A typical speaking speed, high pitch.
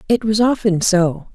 Yes: average, 180 wpm; high, 200 Hz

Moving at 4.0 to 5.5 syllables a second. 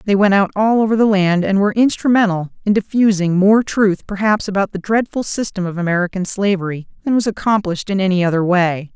No: 5.9 syllables/s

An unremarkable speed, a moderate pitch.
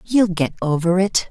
Yes: average, 185 wpm; medium, 180 Hz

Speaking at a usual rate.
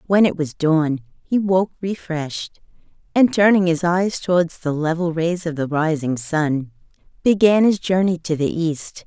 Yes: average, 165 wpm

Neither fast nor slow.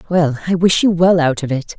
No: fast, 270 wpm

